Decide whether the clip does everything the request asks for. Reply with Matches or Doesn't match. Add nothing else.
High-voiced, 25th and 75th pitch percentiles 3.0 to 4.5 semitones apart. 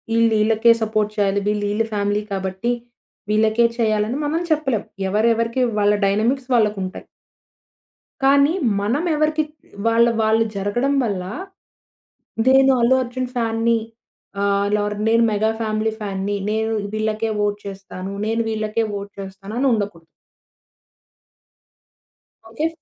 Doesn't match